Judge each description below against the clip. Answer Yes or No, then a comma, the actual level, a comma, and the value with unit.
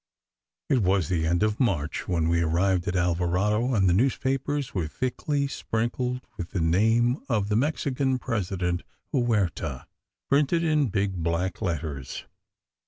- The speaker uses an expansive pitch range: Yes, wide, 6.4 semitones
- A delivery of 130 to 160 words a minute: Yes, average, 140 wpm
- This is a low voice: Yes, low, 100 Hz